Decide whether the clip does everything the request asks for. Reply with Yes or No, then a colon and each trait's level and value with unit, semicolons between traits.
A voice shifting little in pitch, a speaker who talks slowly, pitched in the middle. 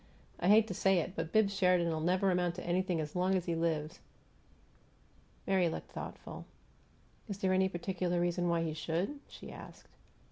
No: narrow, 2.1 semitones; average, 175 wpm; medium, 180 Hz